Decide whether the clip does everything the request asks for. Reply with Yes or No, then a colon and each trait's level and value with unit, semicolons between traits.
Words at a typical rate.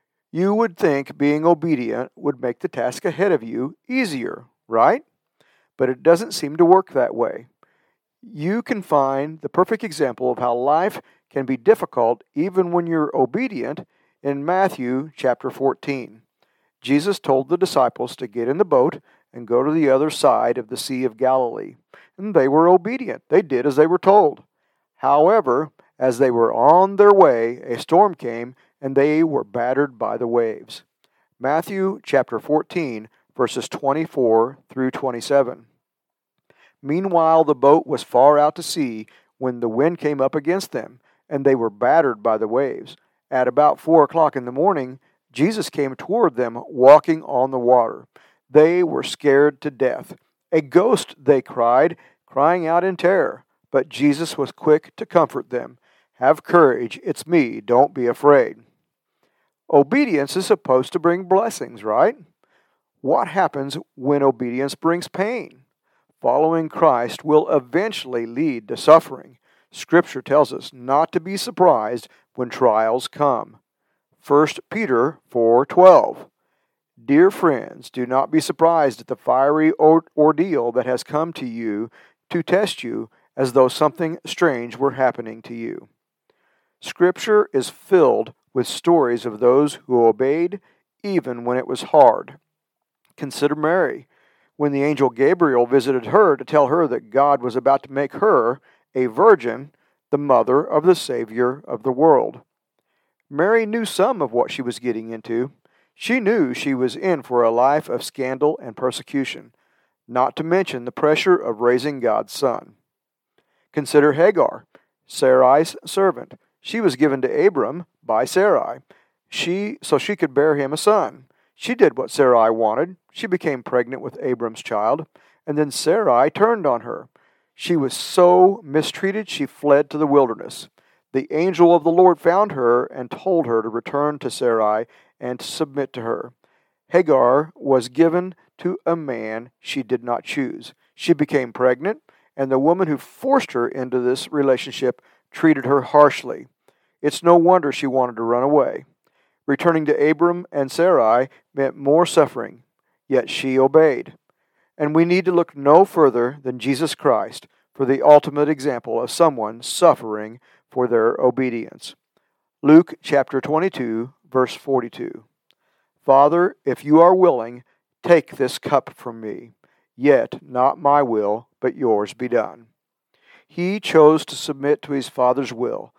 Yes: average, 155 wpm